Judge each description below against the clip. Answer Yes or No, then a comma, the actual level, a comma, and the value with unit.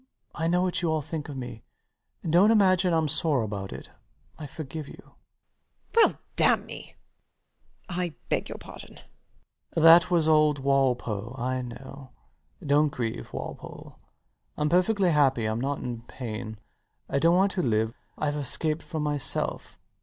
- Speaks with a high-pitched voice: No, medium, 145 Hz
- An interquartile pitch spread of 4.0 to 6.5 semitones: Yes, average, 4.8 semitones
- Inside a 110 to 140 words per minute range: No, average, 160 wpm